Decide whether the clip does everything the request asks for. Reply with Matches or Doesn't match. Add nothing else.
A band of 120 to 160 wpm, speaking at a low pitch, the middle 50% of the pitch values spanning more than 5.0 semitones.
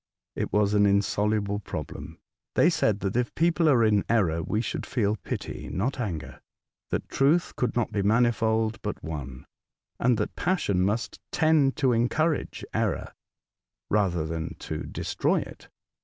Doesn't match